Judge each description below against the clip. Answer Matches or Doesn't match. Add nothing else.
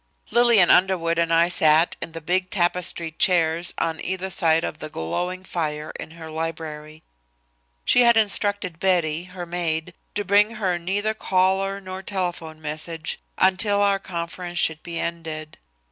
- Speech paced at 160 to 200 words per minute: Doesn't match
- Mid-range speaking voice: Matches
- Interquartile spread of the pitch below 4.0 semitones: Matches